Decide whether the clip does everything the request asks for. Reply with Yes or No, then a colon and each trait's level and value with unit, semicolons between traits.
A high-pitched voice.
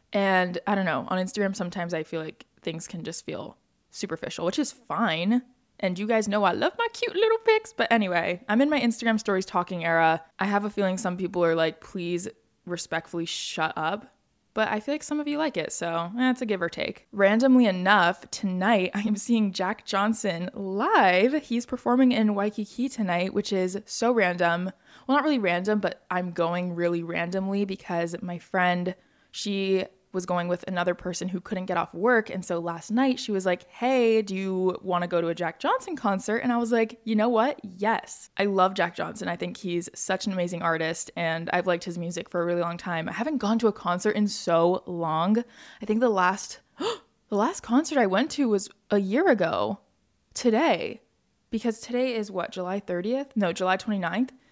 Yes: high, 195 Hz